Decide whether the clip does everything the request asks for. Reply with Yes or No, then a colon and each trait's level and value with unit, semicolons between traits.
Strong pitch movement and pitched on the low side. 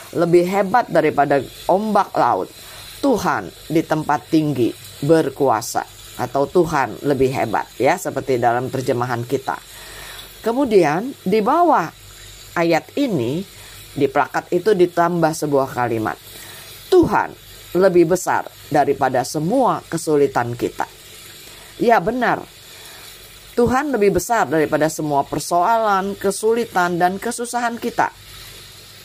No: wide, 6.6 semitones; medium, 155 Hz